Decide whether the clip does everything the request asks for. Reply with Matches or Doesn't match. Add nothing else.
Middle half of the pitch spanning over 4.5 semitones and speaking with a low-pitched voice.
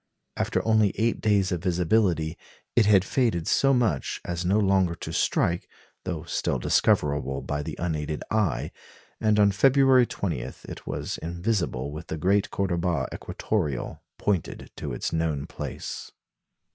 Matches